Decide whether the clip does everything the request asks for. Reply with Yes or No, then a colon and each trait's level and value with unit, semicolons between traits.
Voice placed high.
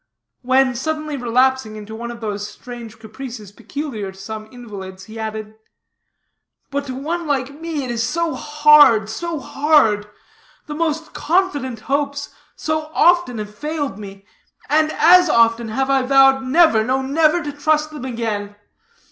Yes: very high, 260 Hz